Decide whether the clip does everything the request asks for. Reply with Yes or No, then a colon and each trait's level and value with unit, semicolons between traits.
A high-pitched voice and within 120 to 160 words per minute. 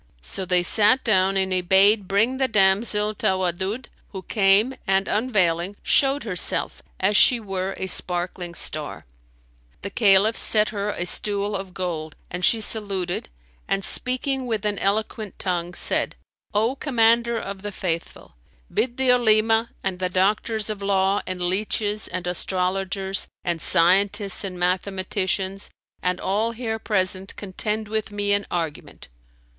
Yes: high, 195 Hz; average, 145 wpm